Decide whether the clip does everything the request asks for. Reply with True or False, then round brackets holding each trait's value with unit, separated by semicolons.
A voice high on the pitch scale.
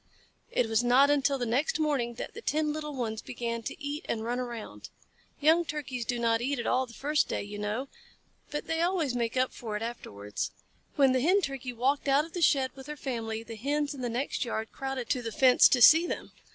True (255 Hz)